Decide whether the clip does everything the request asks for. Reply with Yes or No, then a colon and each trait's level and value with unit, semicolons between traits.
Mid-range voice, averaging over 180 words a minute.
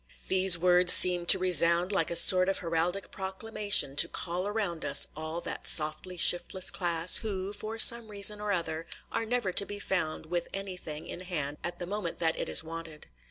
Yes: medium, 180 Hz; average, 190 wpm